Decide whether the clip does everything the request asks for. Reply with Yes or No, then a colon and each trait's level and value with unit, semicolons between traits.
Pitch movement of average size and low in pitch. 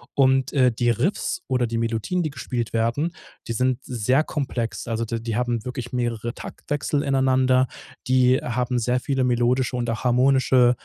No: narrow, 1.9 semitones; low, 125 Hz